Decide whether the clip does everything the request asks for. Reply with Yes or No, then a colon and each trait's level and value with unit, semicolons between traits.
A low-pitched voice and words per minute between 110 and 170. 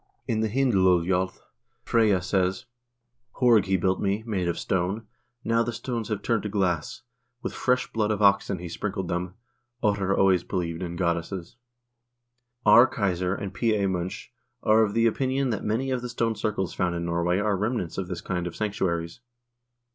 No: low, 100 Hz; average, 185 wpm